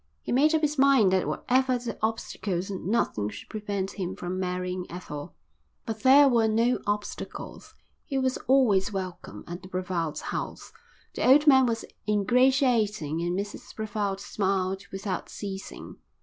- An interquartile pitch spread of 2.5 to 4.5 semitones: No, average, 5.1 semitones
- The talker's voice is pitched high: Yes, high, 205 Hz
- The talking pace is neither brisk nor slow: Yes, average, 150 wpm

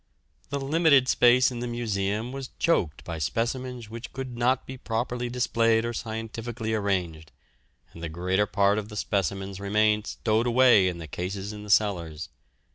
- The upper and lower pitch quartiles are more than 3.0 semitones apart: Yes, average, 3.7 semitones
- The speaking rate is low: No, average, 160 wpm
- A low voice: Yes, low, 110 Hz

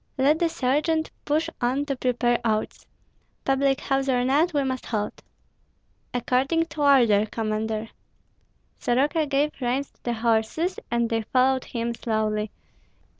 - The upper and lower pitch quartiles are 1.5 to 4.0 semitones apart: Yes, average, 3.7 semitones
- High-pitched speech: Yes, very high, 255 Hz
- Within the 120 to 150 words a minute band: Yes, slow, 135 wpm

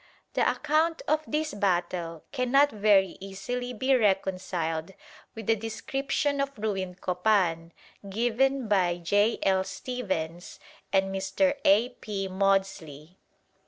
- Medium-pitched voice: No, high, 200 Hz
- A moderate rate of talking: No, slow, 115 wpm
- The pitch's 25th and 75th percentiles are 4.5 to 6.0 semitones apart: Yes, average, 5.1 semitones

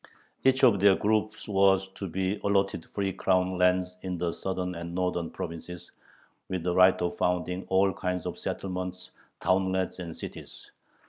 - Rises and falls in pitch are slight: Yes, narrow, 1.2 semitones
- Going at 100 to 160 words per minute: Yes, average, 155 wpm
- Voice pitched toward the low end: Yes, very low, 95 Hz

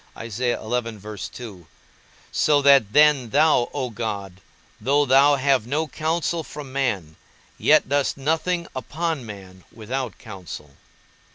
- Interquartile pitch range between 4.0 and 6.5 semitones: Yes, average, 5.2 semitones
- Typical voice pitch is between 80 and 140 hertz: Yes, low, 135 Hz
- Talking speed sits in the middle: No, slow, 105 wpm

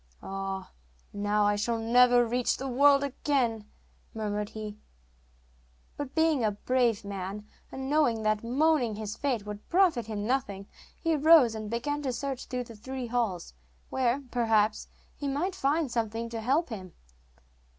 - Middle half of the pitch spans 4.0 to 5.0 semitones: Yes, average, 4.4 semitones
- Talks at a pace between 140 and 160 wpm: Yes, average, 150 wpm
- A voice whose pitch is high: Yes, high, 235 Hz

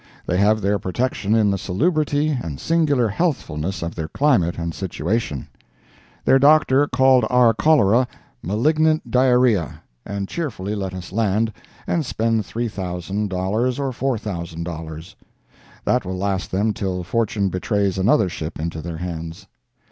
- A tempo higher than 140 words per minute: No, slow, 135 wpm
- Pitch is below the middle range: Yes, low, 105 Hz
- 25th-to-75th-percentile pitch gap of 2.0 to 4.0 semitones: No, wide, 5.6 semitones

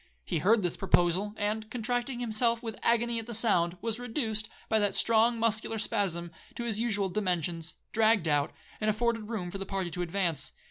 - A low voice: No, high, 215 Hz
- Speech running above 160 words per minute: Yes, average, 185 wpm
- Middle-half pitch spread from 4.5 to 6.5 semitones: No, average, 4.0 semitones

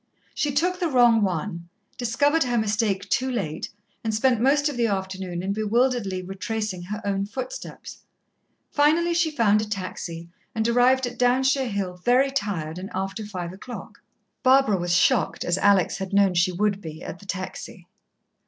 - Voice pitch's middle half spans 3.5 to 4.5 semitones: No, average, 5.1 semitones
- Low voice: No, high, 210 Hz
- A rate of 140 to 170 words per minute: Yes, average, 165 wpm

